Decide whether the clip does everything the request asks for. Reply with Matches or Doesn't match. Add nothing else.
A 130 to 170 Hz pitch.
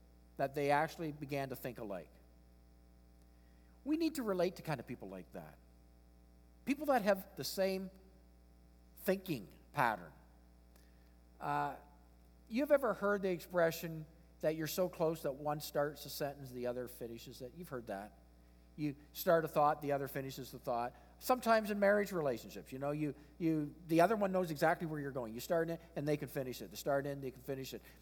Matches